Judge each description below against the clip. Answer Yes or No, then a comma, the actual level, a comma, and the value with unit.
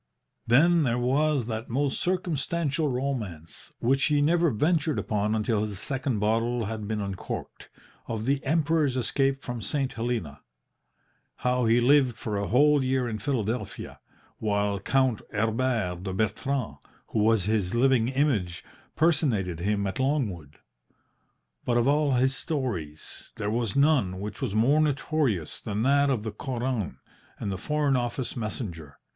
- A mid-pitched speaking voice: No, low, 120 Hz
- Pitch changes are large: No, average, 4.8 semitones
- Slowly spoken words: No, average, 145 wpm